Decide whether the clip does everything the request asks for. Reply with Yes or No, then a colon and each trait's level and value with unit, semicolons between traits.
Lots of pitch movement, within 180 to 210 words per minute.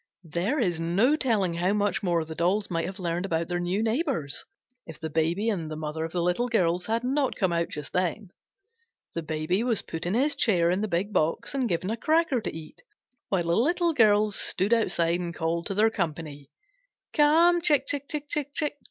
Yes: wide, 5.9 semitones; fast, 205 wpm